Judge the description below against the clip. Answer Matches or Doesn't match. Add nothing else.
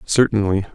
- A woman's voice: Doesn't match